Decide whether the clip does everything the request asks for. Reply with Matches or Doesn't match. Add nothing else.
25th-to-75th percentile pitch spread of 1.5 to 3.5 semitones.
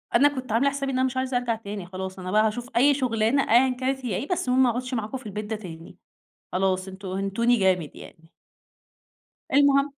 Doesn't match